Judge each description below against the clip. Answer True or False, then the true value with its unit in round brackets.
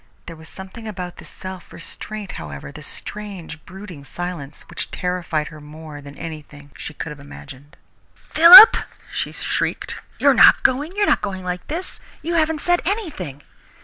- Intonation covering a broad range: True (6.8 semitones)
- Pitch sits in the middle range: True (180 Hz)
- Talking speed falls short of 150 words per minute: False (160 wpm)